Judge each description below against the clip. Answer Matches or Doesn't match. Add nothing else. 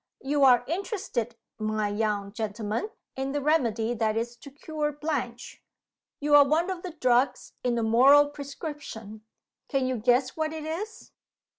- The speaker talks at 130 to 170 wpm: Matches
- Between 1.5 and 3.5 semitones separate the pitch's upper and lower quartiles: Doesn't match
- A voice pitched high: Matches